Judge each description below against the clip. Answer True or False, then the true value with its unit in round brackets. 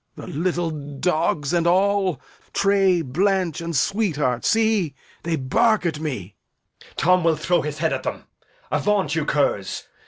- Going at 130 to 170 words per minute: True (155 wpm)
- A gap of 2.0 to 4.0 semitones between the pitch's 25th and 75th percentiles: False (4.4 semitones)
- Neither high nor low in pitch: True (170 Hz)